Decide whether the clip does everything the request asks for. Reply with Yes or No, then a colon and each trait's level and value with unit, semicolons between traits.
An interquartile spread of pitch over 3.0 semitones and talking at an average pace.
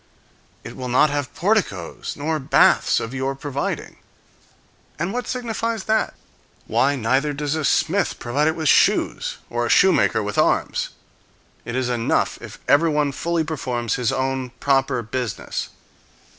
Yes: average, 4.2 semitones; average, 145 wpm